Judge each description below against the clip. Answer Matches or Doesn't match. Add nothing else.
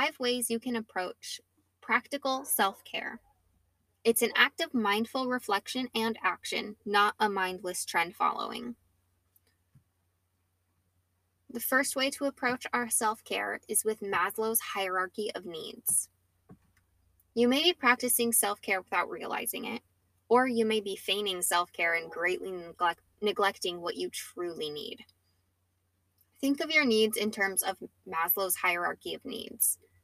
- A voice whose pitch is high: Matches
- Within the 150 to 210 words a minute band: Doesn't match